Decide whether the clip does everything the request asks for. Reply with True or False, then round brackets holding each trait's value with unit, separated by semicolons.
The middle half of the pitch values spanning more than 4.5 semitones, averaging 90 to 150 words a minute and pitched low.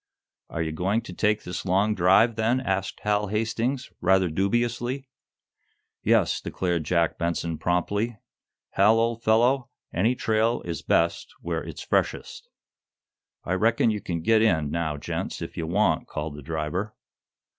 True (4.9 semitones; 145 wpm; 100 Hz)